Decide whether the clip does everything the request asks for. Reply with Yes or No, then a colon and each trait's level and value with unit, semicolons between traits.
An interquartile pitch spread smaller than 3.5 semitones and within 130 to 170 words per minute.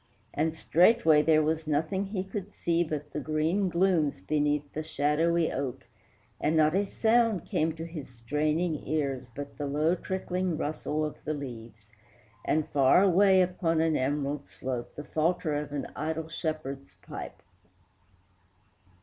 Yes: average, 2.7 semitones; average, 150 wpm